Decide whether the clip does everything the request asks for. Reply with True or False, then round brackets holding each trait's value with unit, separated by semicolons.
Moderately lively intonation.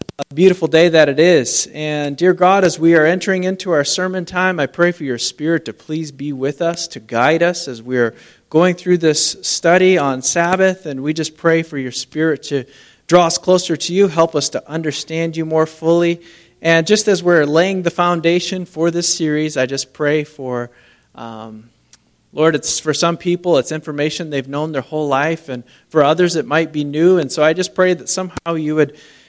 True (3.0 semitones)